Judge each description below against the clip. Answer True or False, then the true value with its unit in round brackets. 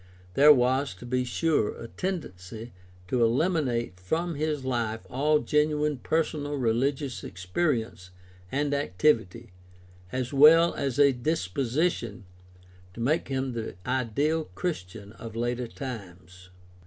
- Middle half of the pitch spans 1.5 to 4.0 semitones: False (4.8 semitones)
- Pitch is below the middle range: True (130 Hz)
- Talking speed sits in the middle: False (115 wpm)